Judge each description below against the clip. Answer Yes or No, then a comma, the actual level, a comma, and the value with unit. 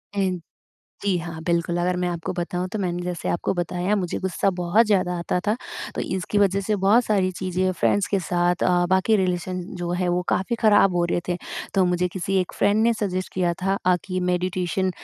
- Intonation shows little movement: Yes, narrow, 1.7 semitones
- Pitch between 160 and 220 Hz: Yes, medium, 185 Hz